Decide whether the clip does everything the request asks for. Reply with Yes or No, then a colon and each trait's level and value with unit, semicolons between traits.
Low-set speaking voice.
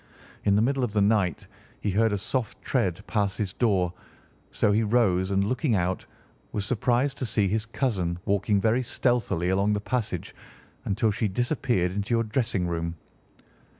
Yes: low, 105 Hz